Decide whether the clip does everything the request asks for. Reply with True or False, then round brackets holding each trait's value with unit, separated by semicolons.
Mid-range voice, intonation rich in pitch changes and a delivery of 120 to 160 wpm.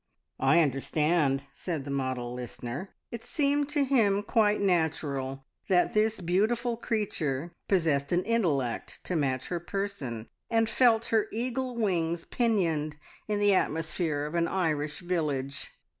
True (175 Hz; 6.8 semitones; 135 wpm)